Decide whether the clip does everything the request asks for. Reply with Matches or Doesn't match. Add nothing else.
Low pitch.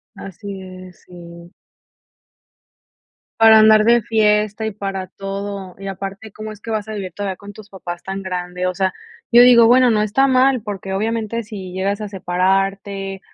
Doesn't match